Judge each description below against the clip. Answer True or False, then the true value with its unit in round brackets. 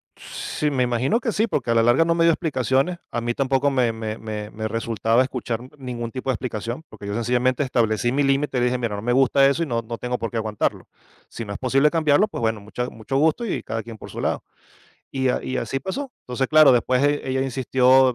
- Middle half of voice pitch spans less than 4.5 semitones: True (2.9 semitones)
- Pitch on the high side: False (125 Hz)